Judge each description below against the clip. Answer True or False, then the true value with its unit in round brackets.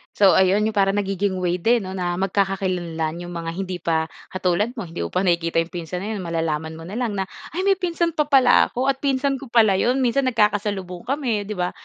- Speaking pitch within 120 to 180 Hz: False (195 Hz)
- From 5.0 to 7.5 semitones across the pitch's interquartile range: True (5.4 semitones)